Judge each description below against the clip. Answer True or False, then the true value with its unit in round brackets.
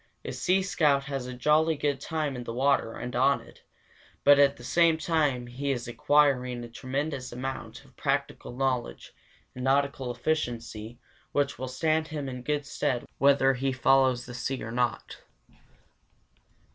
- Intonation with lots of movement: False (2.6 semitones)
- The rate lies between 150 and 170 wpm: True (160 wpm)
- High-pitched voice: False (135 Hz)